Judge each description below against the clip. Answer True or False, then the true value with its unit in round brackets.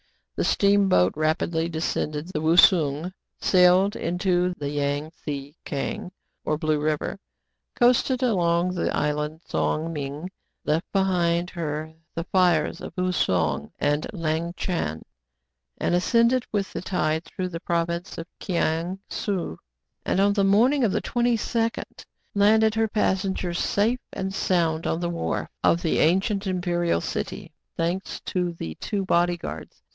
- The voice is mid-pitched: True (175 Hz)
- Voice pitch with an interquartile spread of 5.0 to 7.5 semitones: False (3.6 semitones)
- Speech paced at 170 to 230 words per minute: False (140 wpm)